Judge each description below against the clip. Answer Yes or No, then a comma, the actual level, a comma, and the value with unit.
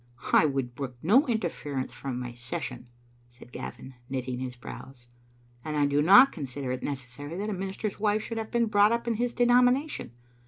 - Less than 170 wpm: No, average, 190 wpm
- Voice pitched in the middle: Yes, medium, 145 Hz